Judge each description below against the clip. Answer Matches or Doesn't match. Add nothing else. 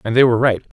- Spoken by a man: Matches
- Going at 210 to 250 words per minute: Doesn't match